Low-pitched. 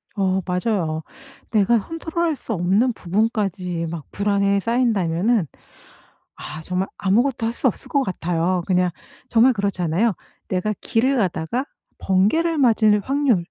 No: high, 200 Hz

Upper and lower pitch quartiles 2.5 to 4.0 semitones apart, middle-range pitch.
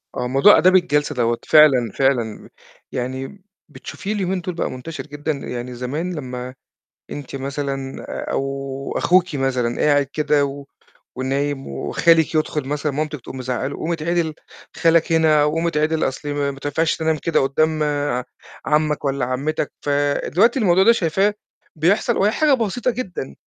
Yes: average, 3.6 semitones; medium, 150 Hz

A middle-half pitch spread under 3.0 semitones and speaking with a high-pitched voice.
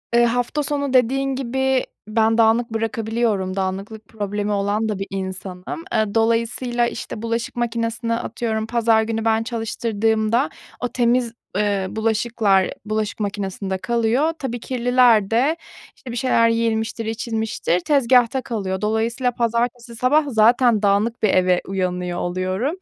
Yes: narrow, 2.5 semitones; high, 225 Hz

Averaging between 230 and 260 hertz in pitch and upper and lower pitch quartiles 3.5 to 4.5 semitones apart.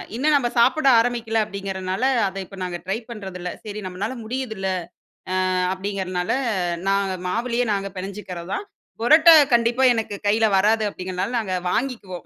No: high, 210 Hz; average, 3.9 semitones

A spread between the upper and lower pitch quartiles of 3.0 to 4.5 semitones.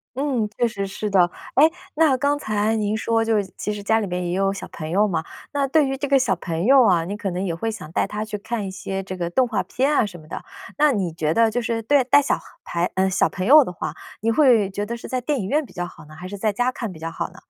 No: average, 5.1 semitones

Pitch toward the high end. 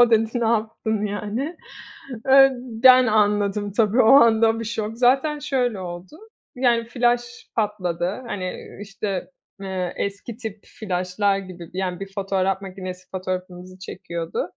Yes: high, 210 Hz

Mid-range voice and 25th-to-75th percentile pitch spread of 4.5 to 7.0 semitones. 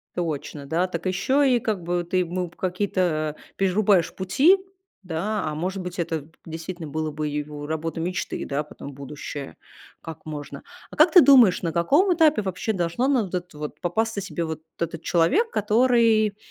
Yes: medium, 180 Hz; average, 5.1 semitones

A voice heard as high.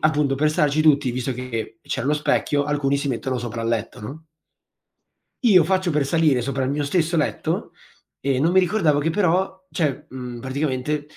No: medium, 145 Hz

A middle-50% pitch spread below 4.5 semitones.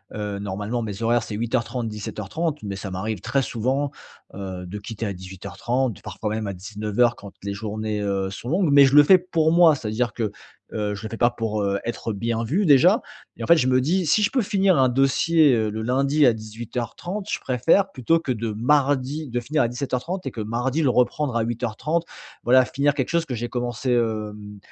No: average, 4.9 semitones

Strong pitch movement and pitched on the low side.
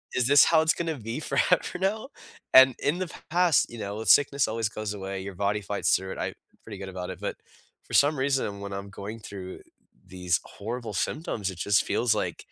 Yes: wide, 6.1 semitones; low, 110 Hz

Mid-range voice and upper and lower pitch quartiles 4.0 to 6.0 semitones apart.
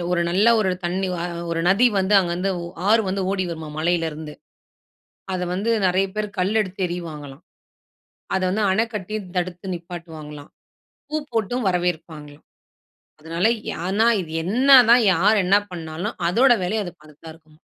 No: medium, 180 Hz; average, 3.6 semitones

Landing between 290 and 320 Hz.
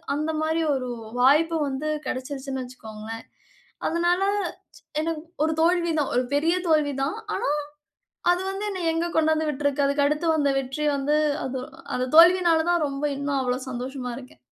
Yes: very high, 295 Hz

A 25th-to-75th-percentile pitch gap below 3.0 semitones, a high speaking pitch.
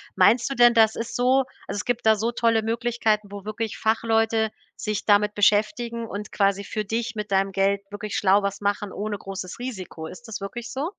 Yes: narrow, 2.4 semitones; high, 215 Hz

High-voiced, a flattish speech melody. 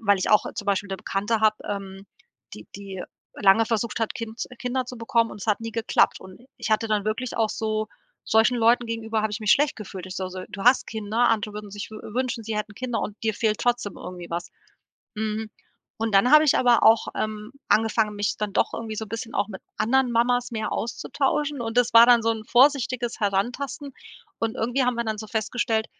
Yes: high, 220 Hz; narrow, 2.3 semitones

